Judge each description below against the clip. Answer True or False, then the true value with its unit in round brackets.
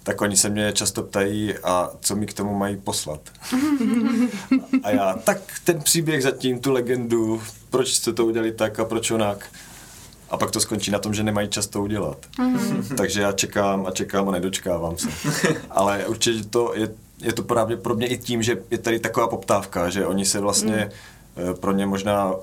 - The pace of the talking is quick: True (190 wpm)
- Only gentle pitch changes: False (3.0 semitones)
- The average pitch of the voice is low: True (110 Hz)